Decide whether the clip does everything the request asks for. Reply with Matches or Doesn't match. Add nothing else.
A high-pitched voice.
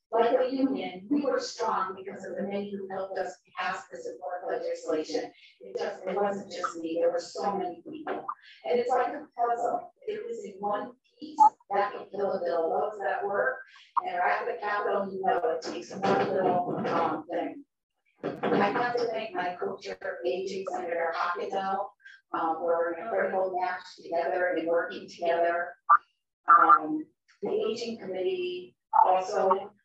Matches